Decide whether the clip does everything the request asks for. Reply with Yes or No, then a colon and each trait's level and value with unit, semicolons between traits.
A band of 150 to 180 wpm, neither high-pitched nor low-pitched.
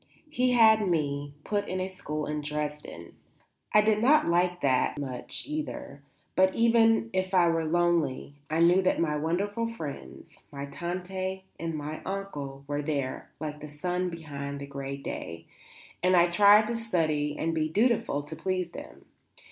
Yes: average, 165 wpm; medium, 170 Hz